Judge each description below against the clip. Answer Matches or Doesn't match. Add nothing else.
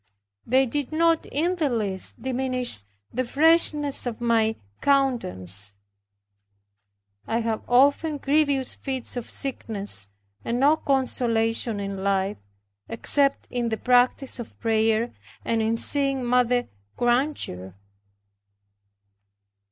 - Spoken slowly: Matches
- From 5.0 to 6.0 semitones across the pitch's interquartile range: Doesn't match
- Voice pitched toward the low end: Doesn't match